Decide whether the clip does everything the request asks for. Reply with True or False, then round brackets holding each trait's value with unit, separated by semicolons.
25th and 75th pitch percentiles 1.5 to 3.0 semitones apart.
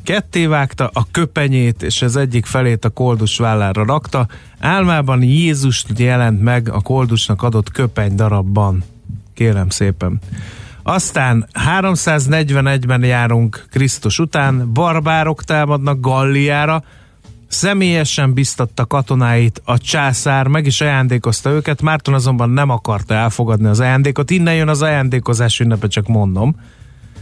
False (4.4 semitones)